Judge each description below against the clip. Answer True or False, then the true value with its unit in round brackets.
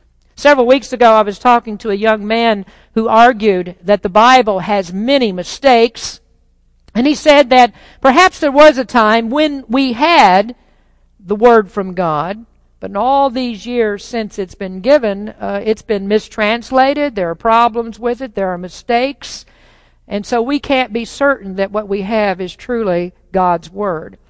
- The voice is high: True (225 Hz)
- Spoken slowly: False (170 wpm)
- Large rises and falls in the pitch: False (4.2 semitones)